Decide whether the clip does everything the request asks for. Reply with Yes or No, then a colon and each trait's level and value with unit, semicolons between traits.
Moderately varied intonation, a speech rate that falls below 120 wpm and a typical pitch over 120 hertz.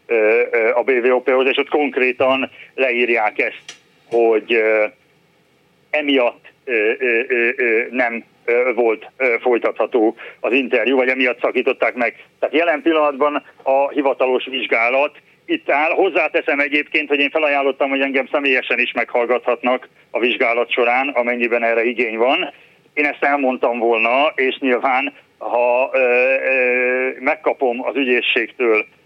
Yes: average, 3.2 semitones; average, 110 wpm; low, 135 Hz